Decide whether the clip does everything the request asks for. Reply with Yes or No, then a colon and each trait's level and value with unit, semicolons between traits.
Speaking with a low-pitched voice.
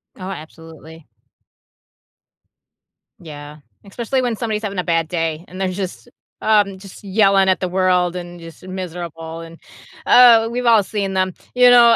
No: medium, 185 Hz